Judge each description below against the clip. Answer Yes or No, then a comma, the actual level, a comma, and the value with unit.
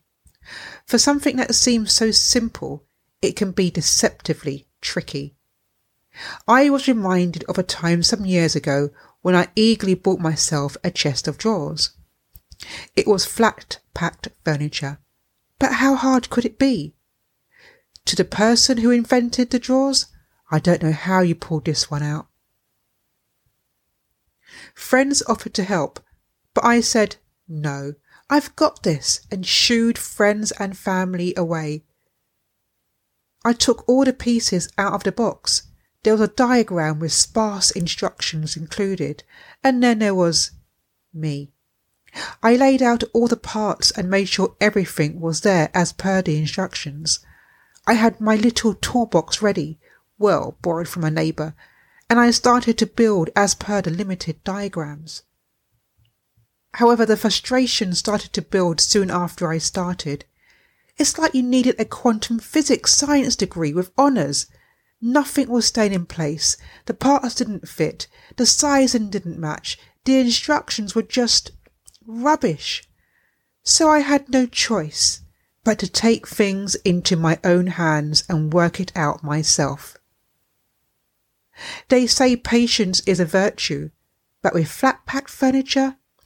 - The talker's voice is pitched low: No, high, 195 Hz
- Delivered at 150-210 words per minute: No, average, 140 wpm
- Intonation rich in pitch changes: Yes, wide, 7.0 semitones